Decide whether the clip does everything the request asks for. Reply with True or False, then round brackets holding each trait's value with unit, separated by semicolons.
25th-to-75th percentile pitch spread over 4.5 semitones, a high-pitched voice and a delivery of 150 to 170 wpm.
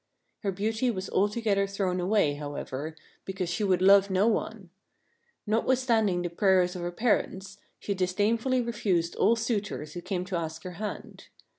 False (3.3 semitones; 195 Hz; 155 wpm)